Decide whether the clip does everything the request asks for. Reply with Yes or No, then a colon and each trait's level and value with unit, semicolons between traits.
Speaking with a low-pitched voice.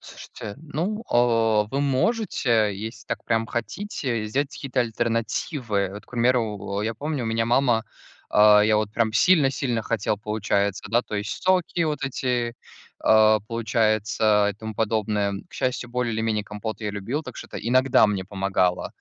Yes: low, 115 Hz